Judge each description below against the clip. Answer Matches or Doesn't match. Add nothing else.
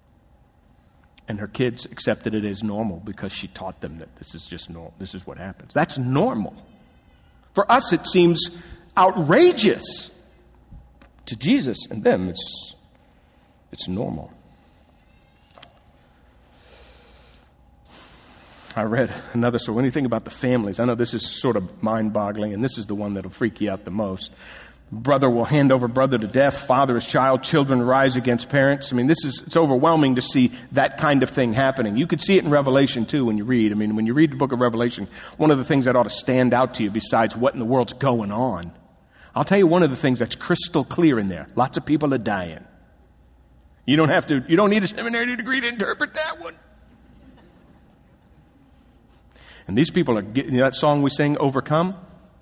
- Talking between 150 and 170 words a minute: Doesn't match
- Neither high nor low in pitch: Doesn't match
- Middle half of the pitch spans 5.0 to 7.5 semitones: Matches